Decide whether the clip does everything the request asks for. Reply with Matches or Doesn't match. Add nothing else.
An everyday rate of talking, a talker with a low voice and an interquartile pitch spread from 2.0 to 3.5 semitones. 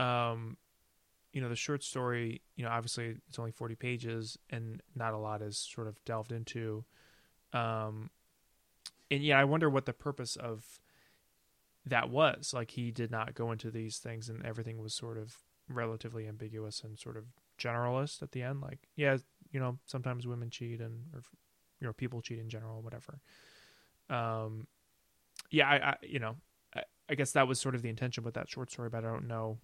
Matches